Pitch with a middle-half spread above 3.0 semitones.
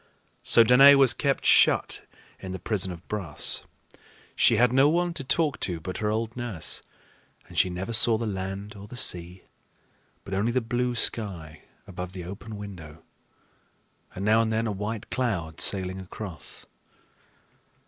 Yes: average, 4.3 semitones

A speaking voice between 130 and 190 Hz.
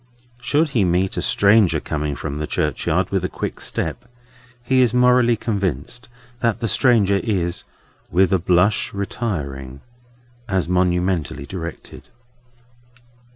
No: very low, 95 Hz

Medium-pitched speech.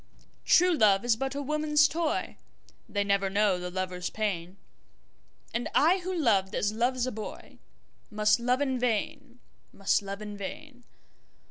No: high, 220 Hz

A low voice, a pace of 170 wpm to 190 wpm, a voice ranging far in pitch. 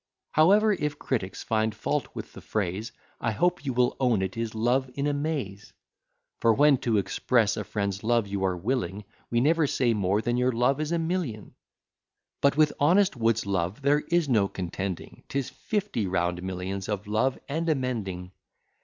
Yes: low, 115 Hz; average, 180 wpm; wide, 6.3 semitones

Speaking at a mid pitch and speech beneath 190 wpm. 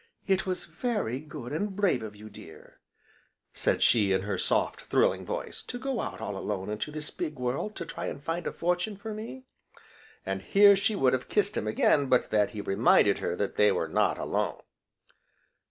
No: medium, 145 Hz; average, 195 wpm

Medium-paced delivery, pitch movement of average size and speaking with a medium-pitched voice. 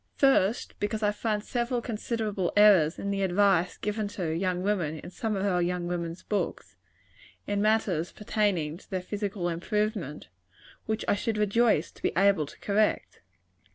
No: average, 160 wpm; average, 3.2 semitones; high, 200 Hz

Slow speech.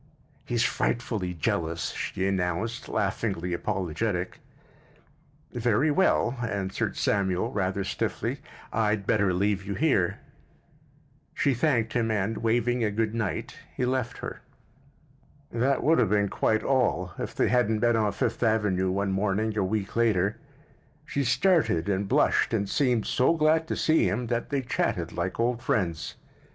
No: average, 145 wpm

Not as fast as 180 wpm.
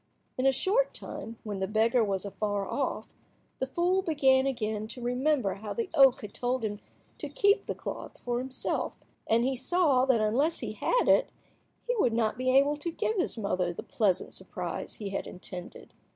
No: average, 190 wpm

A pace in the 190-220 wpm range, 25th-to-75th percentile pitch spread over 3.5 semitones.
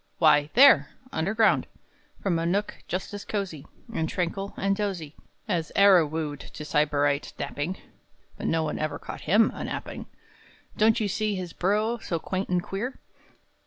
No: average, 155 wpm; average, 4.4 semitones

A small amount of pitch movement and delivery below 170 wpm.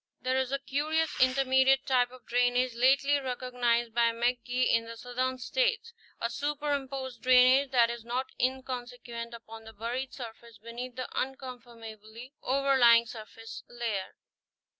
Yes: narrow, 2.0 semitones; average, 140 wpm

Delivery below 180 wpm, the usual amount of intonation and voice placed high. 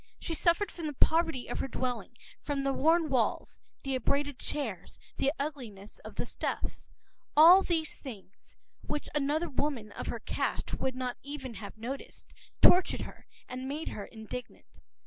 Yes: average, 160 wpm; average, 3.7 semitones; very high, 275 Hz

